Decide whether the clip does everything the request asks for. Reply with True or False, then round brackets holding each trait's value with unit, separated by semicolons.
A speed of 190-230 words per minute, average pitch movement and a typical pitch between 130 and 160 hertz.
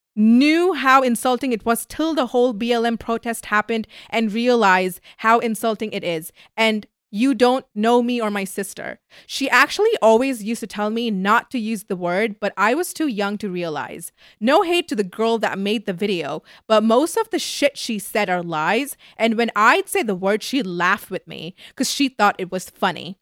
False (200 wpm; 3.7 semitones; 225 Hz)